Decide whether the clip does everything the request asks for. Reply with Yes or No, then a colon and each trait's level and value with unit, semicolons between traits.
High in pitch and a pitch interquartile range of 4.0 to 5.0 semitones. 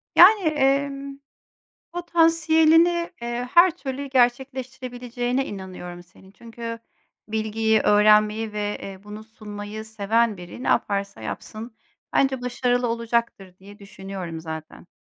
Yes: high, 230 Hz; average, 4.4 semitones